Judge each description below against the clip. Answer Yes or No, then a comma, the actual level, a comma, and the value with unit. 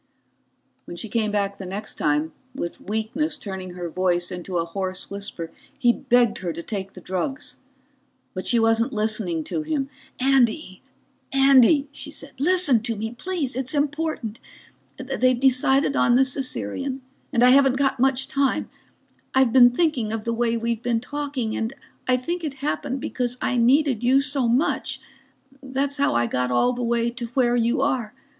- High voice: Yes, high, 245 Hz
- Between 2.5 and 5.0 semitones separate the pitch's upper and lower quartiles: Yes, average, 4.2 semitones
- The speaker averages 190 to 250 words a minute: No, average, 170 wpm